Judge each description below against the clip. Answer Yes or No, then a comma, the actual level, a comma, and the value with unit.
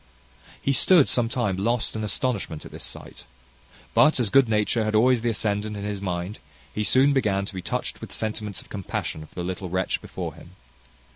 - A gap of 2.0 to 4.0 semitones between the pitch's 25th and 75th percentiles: Yes, average, 3.7 semitones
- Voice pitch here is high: No, low, 105 Hz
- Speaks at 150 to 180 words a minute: No, average, 200 wpm